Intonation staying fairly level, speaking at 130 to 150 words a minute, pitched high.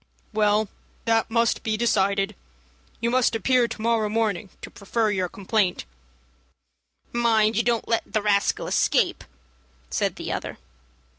Yes: narrow, 2.0 semitones; slow, 135 wpm; high, 220 Hz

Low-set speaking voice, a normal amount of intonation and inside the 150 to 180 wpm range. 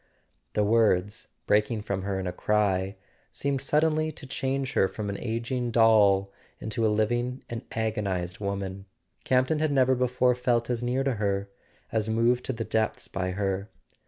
Yes: low, 110 Hz; average, 4.0 semitones; average, 170 wpm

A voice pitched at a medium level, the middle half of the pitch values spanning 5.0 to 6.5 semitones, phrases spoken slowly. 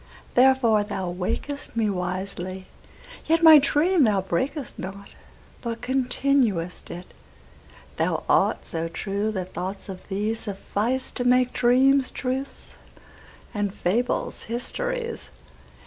No: high, 225 Hz; wide, 5.5 semitones; slow, 100 wpm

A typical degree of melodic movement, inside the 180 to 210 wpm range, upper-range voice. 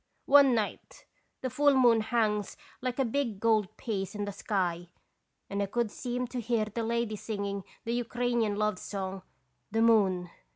No: average, 3.0 semitones; average, 170 wpm; high, 220 Hz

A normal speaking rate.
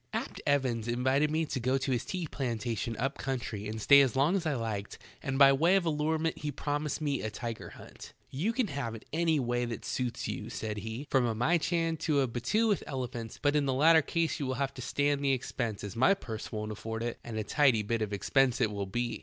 No: fast, 245 wpm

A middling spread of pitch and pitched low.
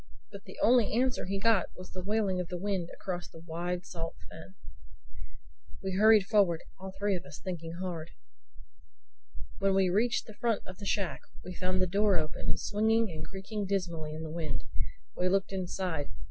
No: average, 3.0 semitones; medium, 185 Hz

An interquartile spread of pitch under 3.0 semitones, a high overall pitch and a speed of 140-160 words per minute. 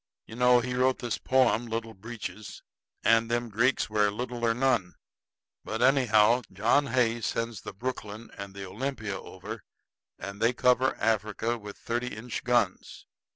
No: narrow, 2.6 semitones; low, 115 Hz; average, 155 wpm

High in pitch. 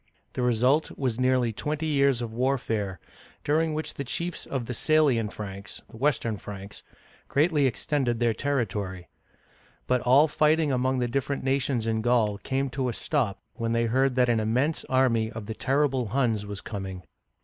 No: low, 125 Hz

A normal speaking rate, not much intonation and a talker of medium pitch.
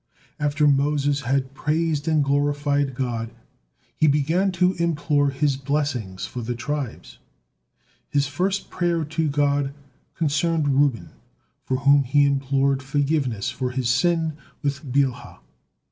No: slow, 125 wpm; narrow, 1.9 semitones; medium, 145 Hz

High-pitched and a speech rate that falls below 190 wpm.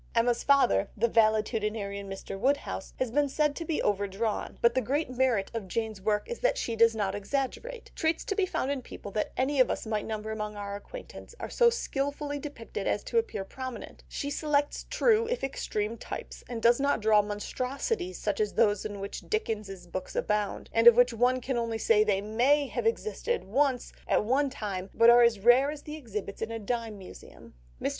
No: high, 235 Hz; average, 200 wpm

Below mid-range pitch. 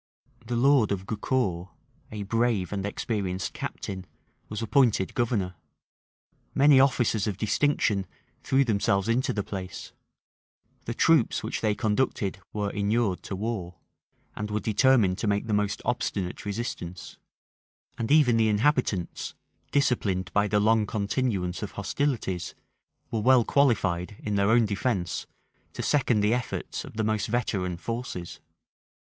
Yes: low, 105 Hz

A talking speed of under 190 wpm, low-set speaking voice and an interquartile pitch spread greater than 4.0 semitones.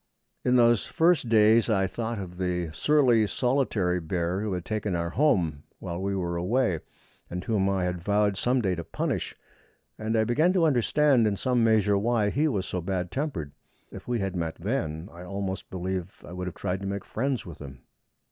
No: average, 195 wpm; low, 100 Hz; average, 4.8 semitones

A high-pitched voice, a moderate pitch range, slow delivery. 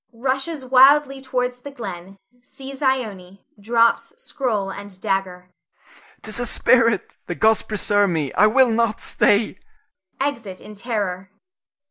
Yes: high, 225 Hz; average, 4.9 semitones; slow, 125 wpm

